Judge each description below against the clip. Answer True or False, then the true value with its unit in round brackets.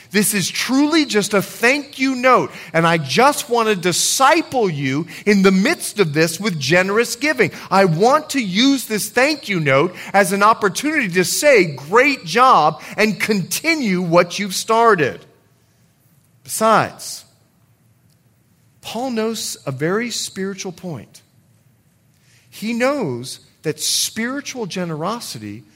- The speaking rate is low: True (130 wpm)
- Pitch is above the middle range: True (200 Hz)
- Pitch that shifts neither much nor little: False (6.1 semitones)